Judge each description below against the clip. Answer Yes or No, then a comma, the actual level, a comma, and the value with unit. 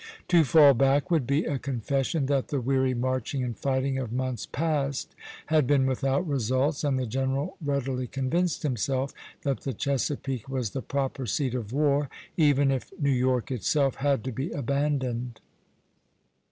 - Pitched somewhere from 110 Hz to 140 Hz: Yes, low, 135 Hz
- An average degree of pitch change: No, narrow, 1.8 semitones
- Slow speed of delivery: No, average, 160 wpm